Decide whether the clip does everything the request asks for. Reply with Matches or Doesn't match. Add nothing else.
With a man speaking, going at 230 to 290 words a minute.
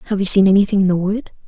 Doesn't match